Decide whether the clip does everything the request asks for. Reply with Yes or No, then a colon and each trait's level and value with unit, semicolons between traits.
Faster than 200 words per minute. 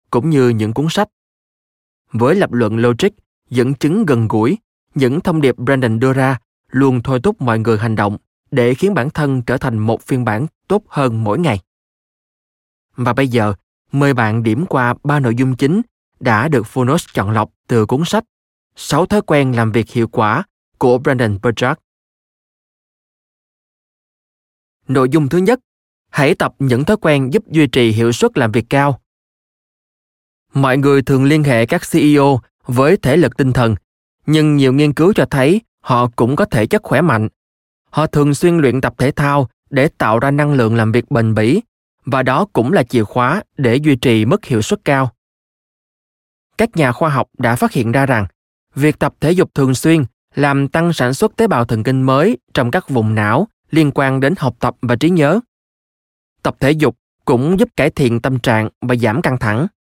No: average, 190 wpm